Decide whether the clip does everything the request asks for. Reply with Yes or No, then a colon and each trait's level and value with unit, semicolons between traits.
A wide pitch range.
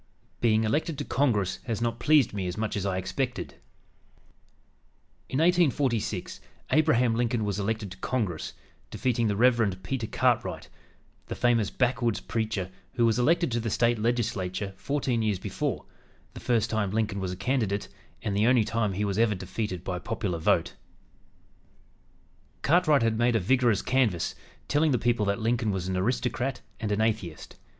No: average, 3.5 semitones